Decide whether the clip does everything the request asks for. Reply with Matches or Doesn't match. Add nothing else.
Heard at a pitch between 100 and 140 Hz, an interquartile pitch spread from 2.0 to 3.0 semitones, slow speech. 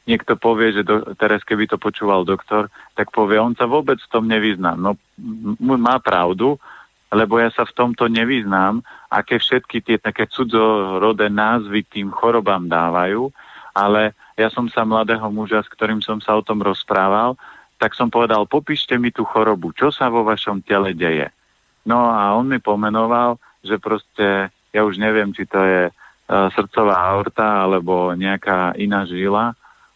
Doesn't match